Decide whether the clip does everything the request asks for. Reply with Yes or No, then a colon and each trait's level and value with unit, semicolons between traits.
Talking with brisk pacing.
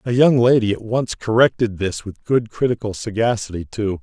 No: average, 180 wpm